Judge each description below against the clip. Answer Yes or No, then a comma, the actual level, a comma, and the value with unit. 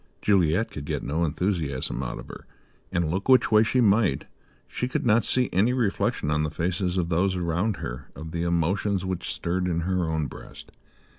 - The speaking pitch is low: Yes, very low, 90 Hz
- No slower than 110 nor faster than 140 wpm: No, average, 195 wpm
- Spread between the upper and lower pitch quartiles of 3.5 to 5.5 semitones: Yes, average, 3.8 semitones